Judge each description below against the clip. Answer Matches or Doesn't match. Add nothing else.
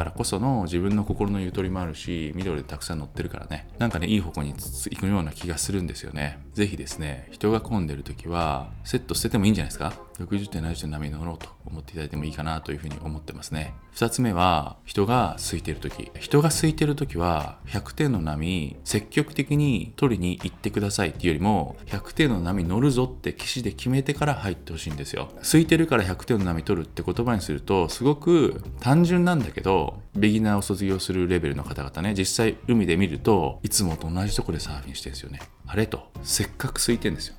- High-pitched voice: Doesn't match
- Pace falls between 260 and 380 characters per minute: Doesn't match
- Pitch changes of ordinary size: Doesn't match